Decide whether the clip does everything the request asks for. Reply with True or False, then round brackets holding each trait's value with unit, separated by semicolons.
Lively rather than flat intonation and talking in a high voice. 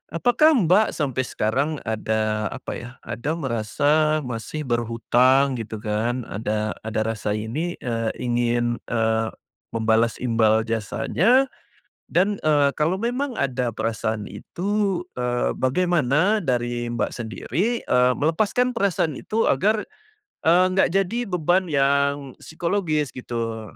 False (7.3 semitones; 130 Hz)